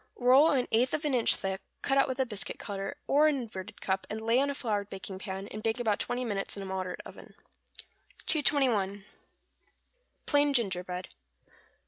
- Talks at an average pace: Yes, average, 180 wpm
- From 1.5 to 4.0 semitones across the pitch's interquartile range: No, average, 5.2 semitones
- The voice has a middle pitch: No, high, 220 Hz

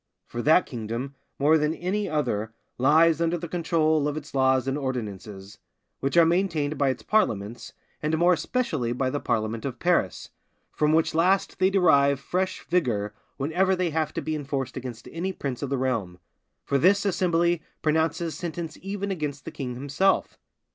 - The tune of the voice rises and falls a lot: No, average, 4.7 semitones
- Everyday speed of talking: Yes, average, 170 wpm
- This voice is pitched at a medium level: Yes, medium, 150 Hz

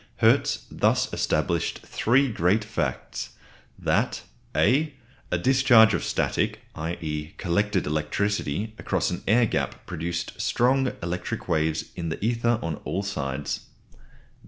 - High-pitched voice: No, very low, 95 Hz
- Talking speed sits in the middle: No, slow, 120 wpm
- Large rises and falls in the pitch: Yes, wide, 6.2 semitones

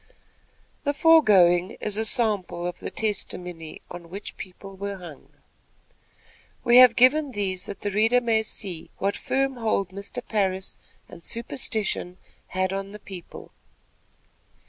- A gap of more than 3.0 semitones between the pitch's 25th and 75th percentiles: Yes, average, 3.7 semitones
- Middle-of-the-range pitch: No, high, 200 Hz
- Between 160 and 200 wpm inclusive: No, slow, 135 wpm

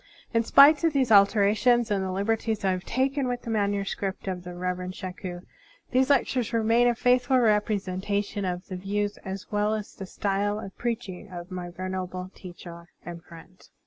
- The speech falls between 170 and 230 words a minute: Yes, average, 175 wpm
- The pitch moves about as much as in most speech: Yes, average, 3.8 semitones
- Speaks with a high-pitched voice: Yes, high, 200 Hz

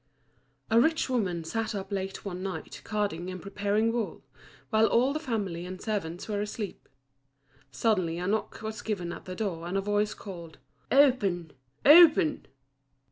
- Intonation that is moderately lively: Yes, average, 3.6 semitones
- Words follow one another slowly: No, average, 155 wpm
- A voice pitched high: Yes, high, 205 Hz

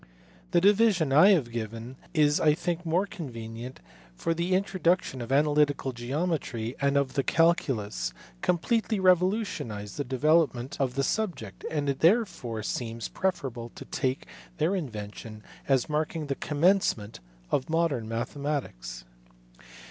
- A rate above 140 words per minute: No, slow, 135 wpm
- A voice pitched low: No, medium, 145 Hz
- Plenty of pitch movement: Yes, wide, 6.3 semitones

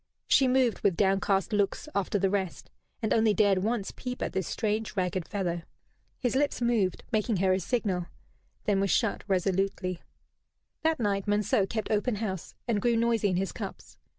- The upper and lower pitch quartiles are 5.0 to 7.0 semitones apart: No, average, 3.0 semitones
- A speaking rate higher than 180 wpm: No, average, 175 wpm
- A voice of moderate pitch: No, high, 205 Hz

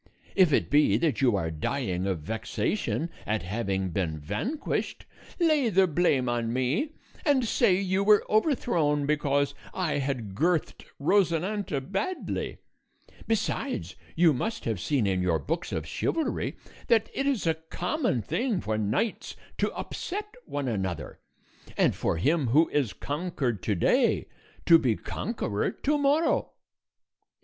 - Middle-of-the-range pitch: Yes, medium, 145 Hz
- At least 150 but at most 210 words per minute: No, average, 140 wpm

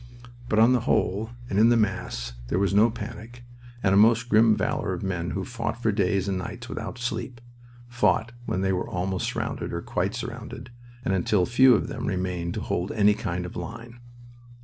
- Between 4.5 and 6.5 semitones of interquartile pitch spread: No, average, 3.8 semitones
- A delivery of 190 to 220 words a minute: Yes, average, 195 wpm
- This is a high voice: No, low, 105 Hz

